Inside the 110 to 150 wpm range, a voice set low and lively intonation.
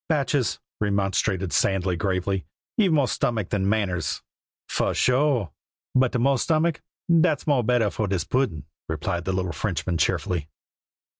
Yes: average, 140 wpm; low, 105 Hz; wide, 6.6 semitones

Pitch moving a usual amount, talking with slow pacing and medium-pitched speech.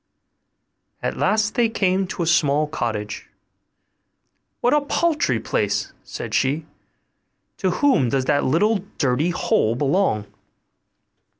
No: wide, 8.2 semitones; slow, 115 wpm; medium, 155 Hz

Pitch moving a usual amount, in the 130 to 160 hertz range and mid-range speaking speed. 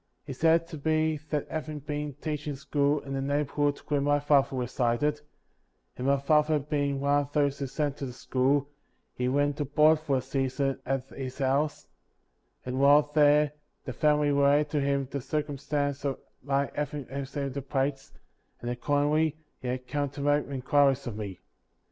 No: narrow, 1.5 semitones; medium, 140 Hz; average, 175 wpm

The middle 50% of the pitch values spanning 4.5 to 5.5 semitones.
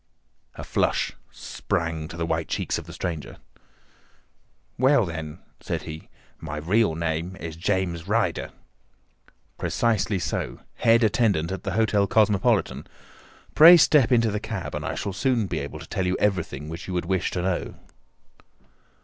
Yes: average, 4.9 semitones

